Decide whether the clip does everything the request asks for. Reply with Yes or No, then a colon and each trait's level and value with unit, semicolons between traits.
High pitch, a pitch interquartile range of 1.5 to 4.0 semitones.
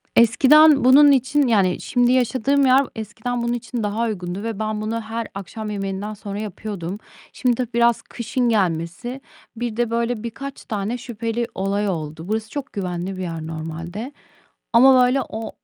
Yes: high, 225 Hz; average, 3.7 semitones